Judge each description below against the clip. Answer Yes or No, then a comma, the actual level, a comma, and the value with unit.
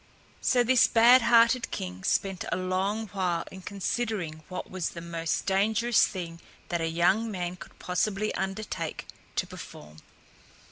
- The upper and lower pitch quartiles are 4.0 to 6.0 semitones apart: Yes, average, 4.3 semitones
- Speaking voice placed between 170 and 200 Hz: Yes, high, 190 Hz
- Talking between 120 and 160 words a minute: Yes, average, 145 wpm